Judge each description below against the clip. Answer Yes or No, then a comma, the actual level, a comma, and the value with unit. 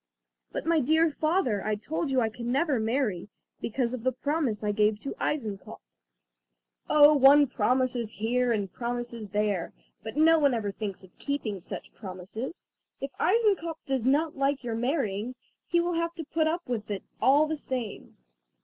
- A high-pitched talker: Yes, very high, 255 Hz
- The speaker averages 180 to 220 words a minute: No, average, 170 wpm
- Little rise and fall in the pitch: No, wide, 5.6 semitones